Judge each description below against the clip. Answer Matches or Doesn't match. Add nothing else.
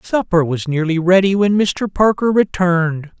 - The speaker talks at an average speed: Matches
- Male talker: Matches